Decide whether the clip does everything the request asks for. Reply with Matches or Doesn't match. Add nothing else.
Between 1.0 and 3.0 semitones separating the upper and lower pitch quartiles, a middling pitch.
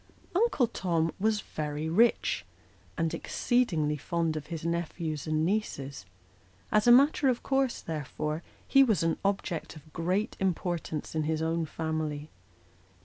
Doesn't match